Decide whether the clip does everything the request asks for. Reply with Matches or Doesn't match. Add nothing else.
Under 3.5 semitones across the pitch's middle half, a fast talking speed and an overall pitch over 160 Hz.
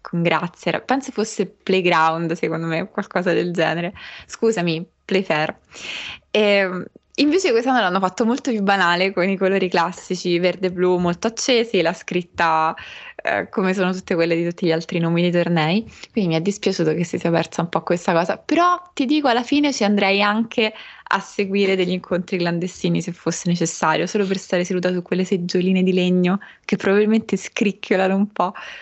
Matches